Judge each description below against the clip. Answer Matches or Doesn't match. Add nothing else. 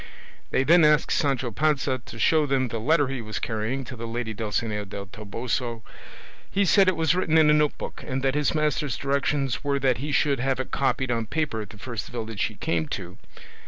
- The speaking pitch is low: Matches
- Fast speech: Matches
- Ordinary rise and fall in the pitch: Matches